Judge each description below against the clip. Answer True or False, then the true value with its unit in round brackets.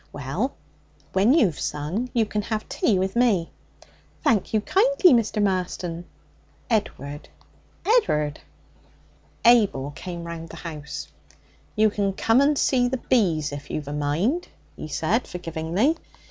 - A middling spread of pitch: False (6.8 semitones)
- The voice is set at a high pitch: True (195 Hz)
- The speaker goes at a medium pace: False (130 wpm)